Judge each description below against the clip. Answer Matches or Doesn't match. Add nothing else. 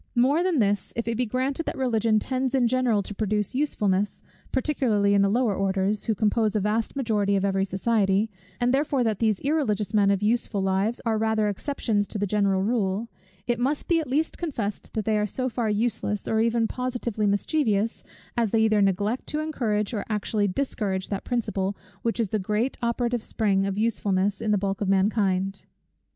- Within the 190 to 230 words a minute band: Matches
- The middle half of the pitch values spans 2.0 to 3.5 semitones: Matches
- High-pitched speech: Matches